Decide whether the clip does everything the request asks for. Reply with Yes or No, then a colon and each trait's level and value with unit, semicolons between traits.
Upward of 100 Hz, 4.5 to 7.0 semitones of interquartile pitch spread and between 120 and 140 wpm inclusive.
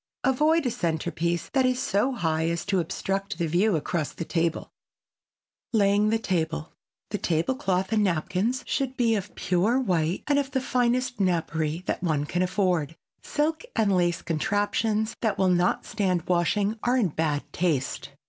No: high, 190 Hz; average, 5.0 semitones; average, 165 wpm